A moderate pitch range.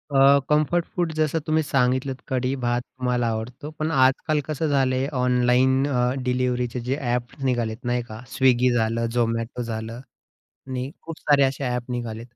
No: narrow, 2.2 semitones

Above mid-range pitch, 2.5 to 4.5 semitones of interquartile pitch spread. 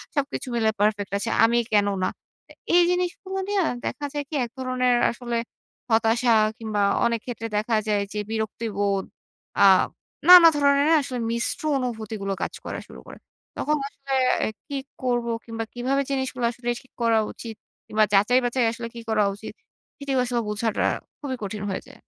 Yes: high, 235 Hz; average, 3.5 semitones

